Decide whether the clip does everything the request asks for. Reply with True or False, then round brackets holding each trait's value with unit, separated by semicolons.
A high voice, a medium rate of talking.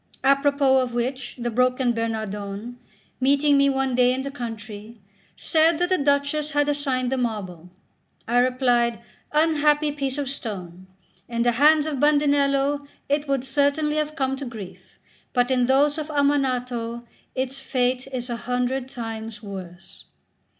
True (260 Hz; 150 wpm)